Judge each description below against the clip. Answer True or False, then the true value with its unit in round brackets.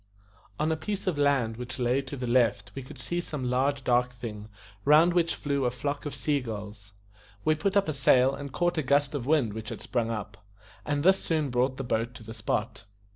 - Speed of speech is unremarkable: False (225 wpm)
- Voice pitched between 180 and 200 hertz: False (130 Hz)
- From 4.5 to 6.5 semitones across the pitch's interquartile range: False (3.8 semitones)